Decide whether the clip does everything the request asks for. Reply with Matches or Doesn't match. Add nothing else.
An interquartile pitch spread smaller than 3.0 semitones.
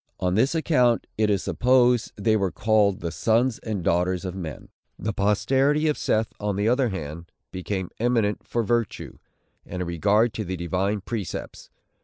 Doesn't match